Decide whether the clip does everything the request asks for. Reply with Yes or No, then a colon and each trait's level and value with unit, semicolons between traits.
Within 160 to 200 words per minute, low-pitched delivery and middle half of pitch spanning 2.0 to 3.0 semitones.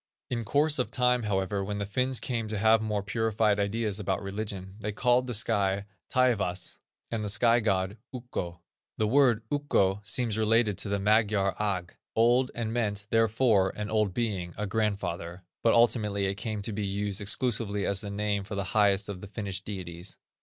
Yes: average, 180 wpm; low, 105 Hz; narrow, 2.5 semitones